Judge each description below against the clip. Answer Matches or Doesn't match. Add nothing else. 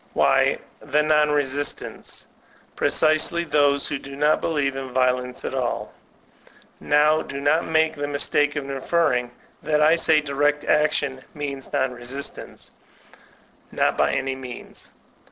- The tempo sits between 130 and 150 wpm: Matches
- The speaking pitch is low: Doesn't match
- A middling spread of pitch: Doesn't match